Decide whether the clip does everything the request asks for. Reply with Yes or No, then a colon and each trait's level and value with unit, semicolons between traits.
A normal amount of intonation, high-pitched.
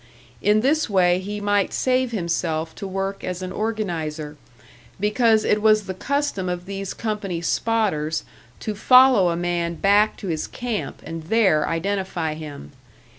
Yes: average, 4.1 semitones; high, 195 Hz